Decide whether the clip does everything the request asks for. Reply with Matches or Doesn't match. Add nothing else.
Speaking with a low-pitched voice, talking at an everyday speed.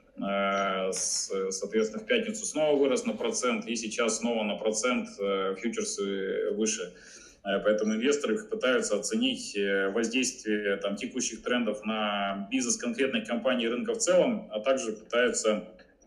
Matches